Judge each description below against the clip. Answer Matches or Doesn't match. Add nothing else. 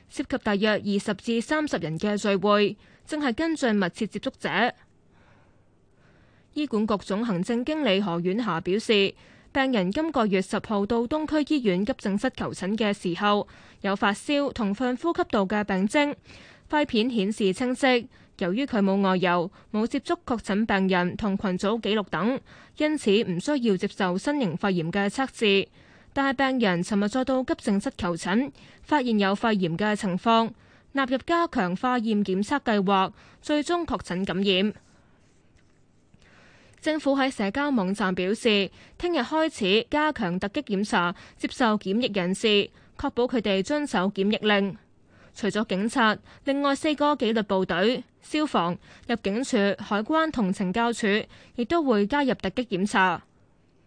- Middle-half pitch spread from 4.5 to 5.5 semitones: Matches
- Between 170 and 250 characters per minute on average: Matches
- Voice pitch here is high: Matches